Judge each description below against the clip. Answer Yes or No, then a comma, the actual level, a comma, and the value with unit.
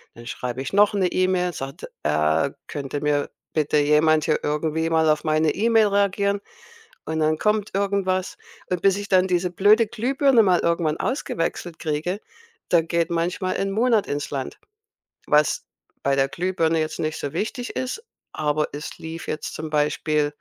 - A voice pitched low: No, medium, 165 Hz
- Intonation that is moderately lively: Yes, average, 4.6 semitones